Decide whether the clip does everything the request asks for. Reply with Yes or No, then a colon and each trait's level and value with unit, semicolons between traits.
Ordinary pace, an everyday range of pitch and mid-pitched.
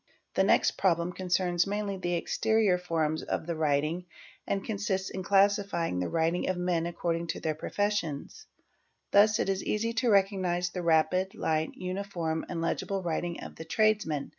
Yes: average, 165 wpm; average, 3.1 semitones; medium, 180 Hz